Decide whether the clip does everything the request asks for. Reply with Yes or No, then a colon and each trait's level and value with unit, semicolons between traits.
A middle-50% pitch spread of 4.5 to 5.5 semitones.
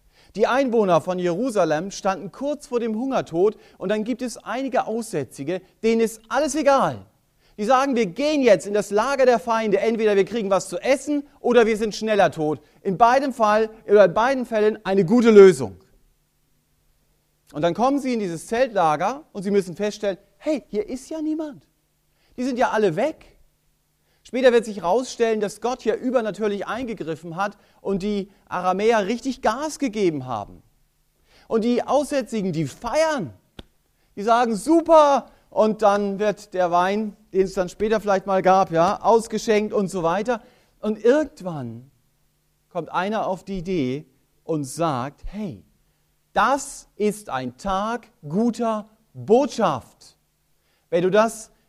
Yes: average, 4.8 semitones